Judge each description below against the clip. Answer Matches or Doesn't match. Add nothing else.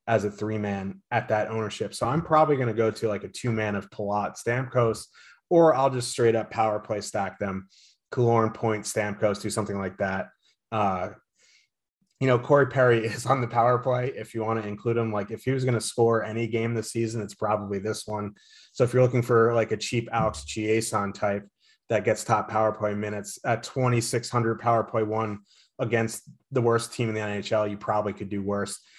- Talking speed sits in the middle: Doesn't match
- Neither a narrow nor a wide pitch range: Doesn't match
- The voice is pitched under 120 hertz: Matches